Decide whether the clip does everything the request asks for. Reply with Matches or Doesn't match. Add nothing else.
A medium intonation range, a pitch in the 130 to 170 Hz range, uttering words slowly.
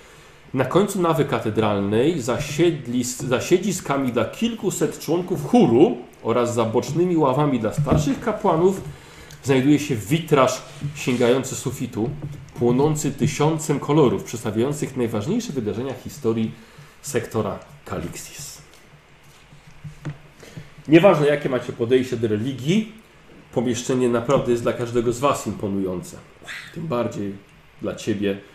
Matches